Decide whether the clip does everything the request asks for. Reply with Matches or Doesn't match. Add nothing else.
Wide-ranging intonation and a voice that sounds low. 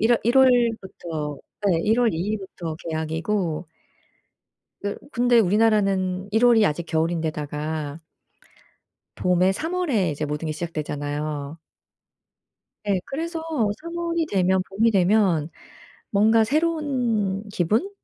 Doesn't match